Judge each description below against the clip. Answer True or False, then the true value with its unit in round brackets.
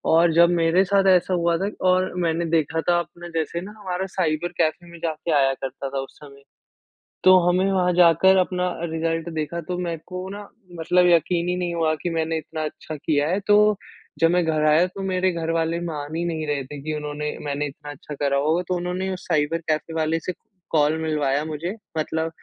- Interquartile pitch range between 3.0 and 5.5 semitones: False (2.6 semitones)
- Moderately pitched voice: True (165 Hz)